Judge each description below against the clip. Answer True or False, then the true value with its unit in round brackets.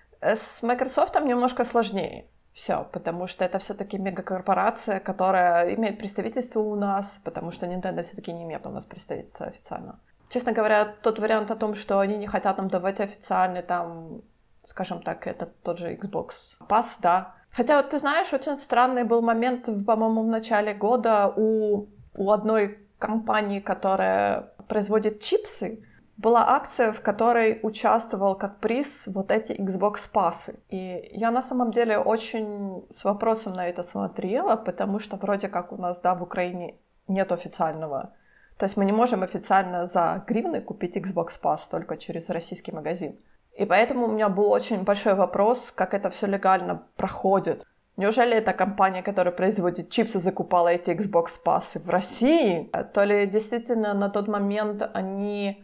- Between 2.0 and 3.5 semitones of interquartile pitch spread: True (3.1 semitones)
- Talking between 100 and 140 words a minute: False (155 wpm)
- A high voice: True (205 Hz)